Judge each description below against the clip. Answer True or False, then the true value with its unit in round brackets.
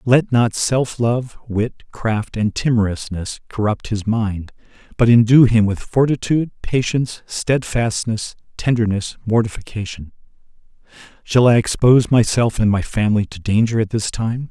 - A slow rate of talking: True (130 wpm)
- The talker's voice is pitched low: True (115 Hz)